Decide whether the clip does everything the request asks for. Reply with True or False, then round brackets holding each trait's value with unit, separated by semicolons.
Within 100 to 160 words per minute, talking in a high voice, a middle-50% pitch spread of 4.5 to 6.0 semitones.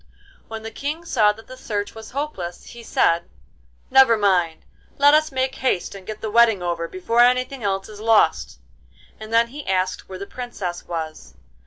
False (180 wpm; 220 Hz; 5.2 semitones)